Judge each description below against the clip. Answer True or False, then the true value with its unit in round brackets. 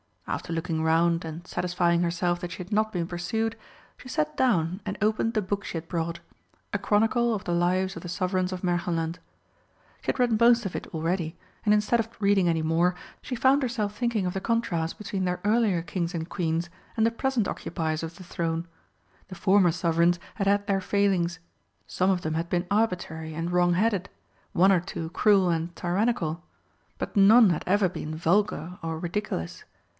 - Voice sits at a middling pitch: True (180 Hz)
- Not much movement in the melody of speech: False (3.6 semitones)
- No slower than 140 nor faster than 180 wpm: False (190 wpm)